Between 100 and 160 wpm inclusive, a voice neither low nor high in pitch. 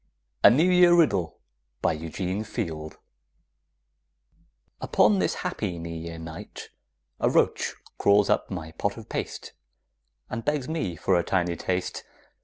No: slow, 135 wpm; very low, 90 Hz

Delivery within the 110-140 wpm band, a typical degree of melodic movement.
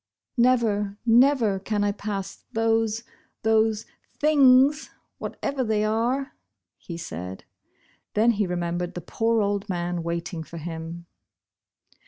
Yes: slow, 135 wpm; average, 4.7 semitones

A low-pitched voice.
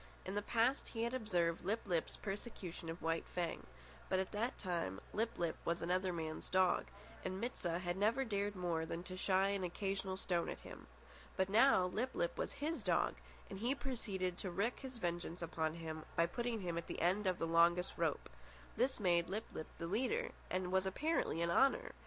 No: medium, 185 Hz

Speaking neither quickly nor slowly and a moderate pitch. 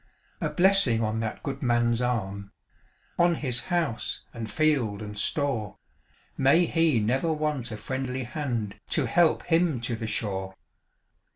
No: average, 145 wpm; low, 125 Hz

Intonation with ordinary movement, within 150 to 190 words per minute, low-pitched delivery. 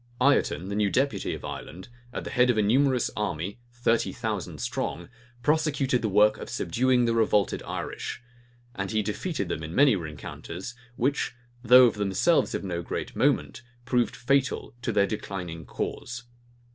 Yes: average, 4.2 semitones; average, 160 wpm; low, 115 Hz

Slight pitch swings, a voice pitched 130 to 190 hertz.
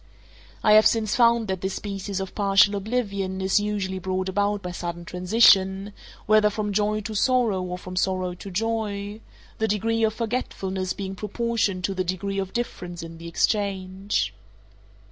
No: narrow, 2.3 semitones; high, 200 Hz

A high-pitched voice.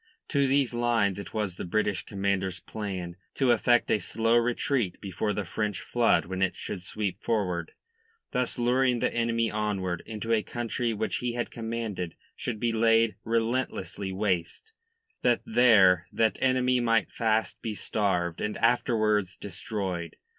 No: low, 110 Hz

